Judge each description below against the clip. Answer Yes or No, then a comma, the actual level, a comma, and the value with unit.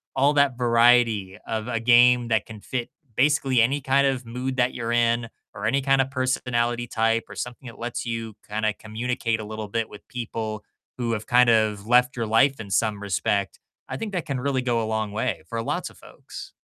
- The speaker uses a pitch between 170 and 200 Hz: No, low, 120 Hz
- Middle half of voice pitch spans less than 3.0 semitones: Yes, narrow, 2.4 semitones